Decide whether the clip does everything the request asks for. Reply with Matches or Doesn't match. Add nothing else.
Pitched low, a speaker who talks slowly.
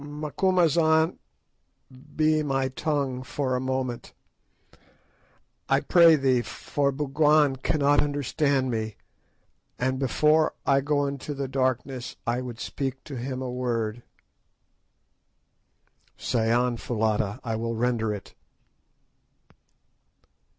Matches